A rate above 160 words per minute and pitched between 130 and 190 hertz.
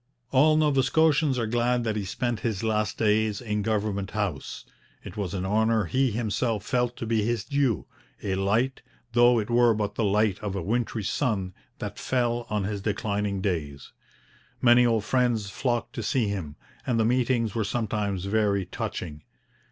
No: average, 175 wpm; low, 110 Hz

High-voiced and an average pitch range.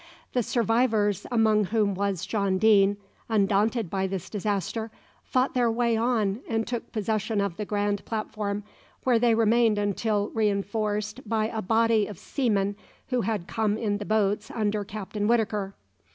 No: high, 215 Hz; narrow, 1.9 semitones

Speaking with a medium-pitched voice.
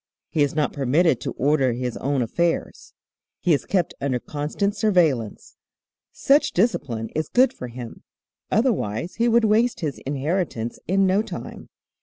Yes: medium, 155 Hz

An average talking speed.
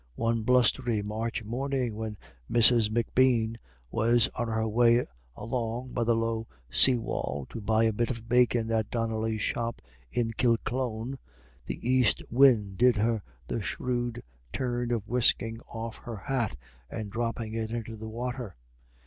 Yes: average, 150 wpm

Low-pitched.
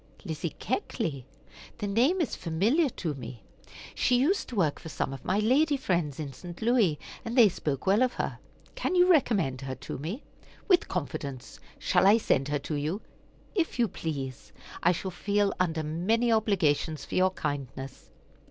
No: medium, 180 Hz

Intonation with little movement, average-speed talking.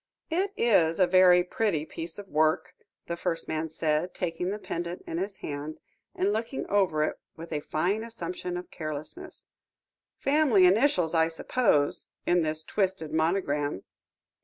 No: average, 3.8 semitones; average, 150 wpm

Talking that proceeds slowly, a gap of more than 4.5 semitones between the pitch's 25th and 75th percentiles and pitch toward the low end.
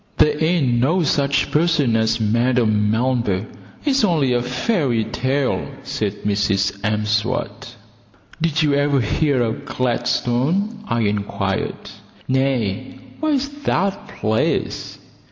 Yes: slow, 115 wpm; average, 5.2 semitones; low, 125 Hz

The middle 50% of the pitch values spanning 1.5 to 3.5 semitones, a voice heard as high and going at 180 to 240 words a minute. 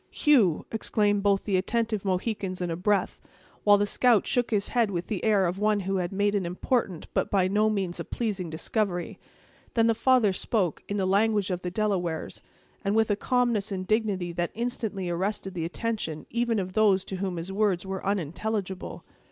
Yes: average, 2.8 semitones; high, 200 Hz; average, 195 wpm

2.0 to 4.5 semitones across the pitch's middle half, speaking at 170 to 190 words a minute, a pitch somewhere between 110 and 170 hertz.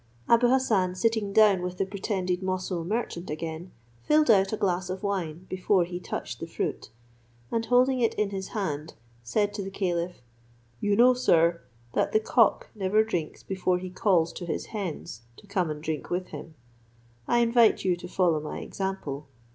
No: average, 3.5 semitones; average, 180 wpm; high, 190 Hz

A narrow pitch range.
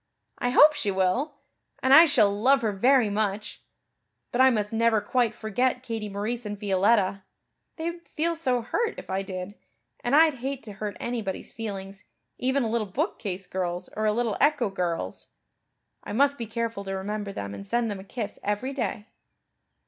No: average, 4.3 semitones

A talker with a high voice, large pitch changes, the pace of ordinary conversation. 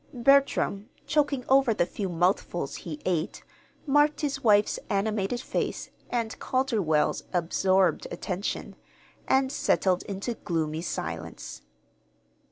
No: high, 200 Hz; wide, 6.5 semitones; slow, 105 wpm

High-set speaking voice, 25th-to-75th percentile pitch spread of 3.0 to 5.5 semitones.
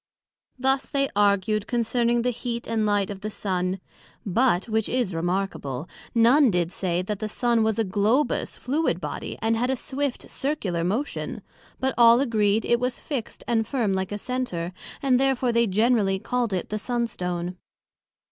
Yes: high, 225 Hz; average, 4.3 semitones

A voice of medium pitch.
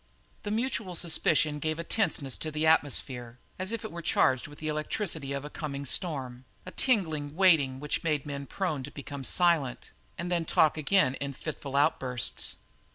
Yes: medium, 150 Hz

